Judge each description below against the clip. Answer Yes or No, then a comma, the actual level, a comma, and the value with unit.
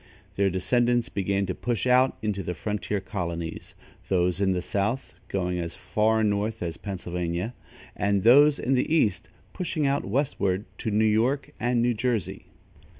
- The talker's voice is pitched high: No, low, 105 Hz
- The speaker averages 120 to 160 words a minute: Yes, average, 155 wpm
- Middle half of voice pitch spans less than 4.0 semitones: No, average, 4.6 semitones